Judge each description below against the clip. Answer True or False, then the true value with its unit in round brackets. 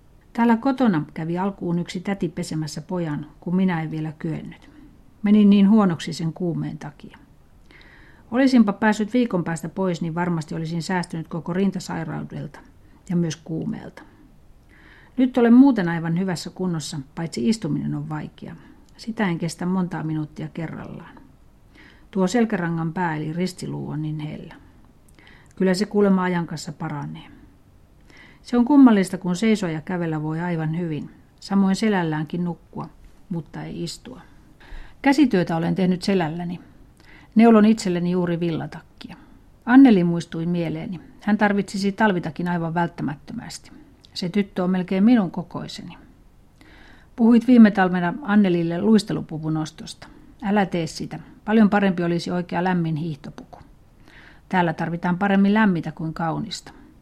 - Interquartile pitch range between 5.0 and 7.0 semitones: False (3.6 semitones)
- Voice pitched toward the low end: False (180 Hz)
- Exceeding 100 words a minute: True (130 wpm)